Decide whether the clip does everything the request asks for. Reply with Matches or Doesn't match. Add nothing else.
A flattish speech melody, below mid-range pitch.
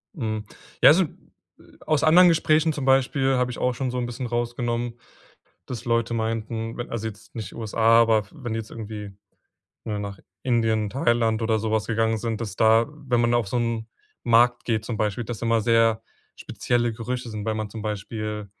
Matches